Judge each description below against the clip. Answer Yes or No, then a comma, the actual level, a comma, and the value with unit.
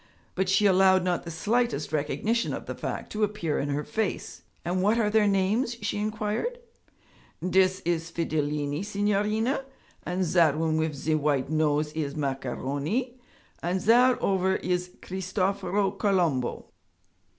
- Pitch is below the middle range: No, medium, 185 Hz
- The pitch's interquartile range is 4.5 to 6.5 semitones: Yes, average, 5.0 semitones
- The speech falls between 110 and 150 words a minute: Yes, average, 140 wpm